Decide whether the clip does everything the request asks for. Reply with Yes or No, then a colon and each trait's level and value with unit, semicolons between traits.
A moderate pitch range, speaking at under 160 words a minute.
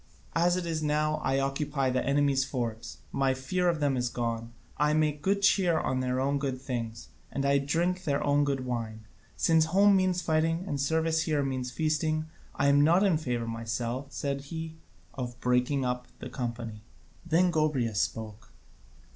No: average, 4.2 semitones; average, 175 wpm